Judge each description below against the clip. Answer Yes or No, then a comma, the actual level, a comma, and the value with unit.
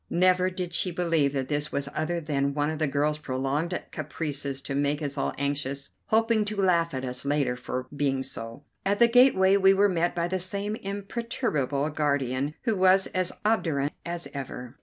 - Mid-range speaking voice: Yes, medium, 155 Hz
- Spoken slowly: No, average, 190 wpm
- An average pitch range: Yes, average, 4.9 semitones